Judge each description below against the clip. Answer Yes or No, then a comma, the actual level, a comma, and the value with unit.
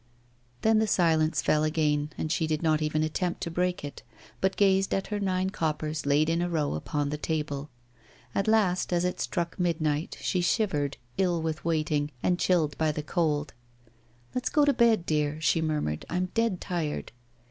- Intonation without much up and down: No, average, 3.1 semitones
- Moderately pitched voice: Yes, medium, 160 Hz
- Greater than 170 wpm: Yes, average, 180 wpm